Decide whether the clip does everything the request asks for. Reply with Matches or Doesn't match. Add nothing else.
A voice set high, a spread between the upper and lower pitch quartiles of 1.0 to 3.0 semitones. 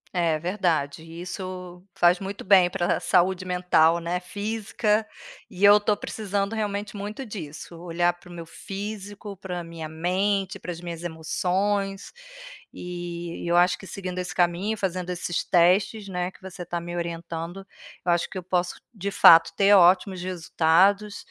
Doesn't match